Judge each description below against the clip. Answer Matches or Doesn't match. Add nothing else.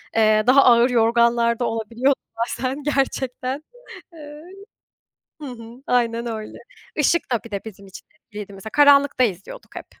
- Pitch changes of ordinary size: Matches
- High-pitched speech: Matches